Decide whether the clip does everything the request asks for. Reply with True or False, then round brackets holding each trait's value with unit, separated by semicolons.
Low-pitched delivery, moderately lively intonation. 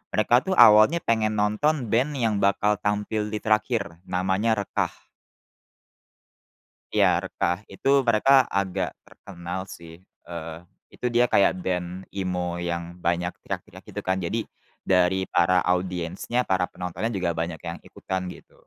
True (95 Hz; 3.5 semitones)